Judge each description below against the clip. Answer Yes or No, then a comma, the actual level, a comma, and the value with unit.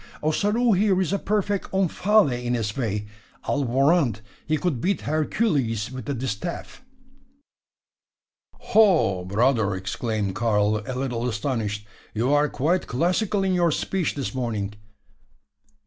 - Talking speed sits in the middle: No, slow, 130 wpm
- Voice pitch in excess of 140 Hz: No, low, 135 Hz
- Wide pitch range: Yes, wide, 8.2 semitones